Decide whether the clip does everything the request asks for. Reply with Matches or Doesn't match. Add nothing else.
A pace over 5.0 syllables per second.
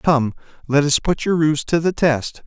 Doesn't match